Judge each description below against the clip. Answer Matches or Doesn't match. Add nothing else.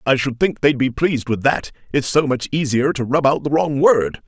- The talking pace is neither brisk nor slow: Doesn't match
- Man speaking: Matches